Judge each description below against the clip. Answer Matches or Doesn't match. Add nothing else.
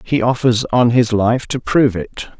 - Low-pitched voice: Matches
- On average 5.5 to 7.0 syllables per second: Doesn't match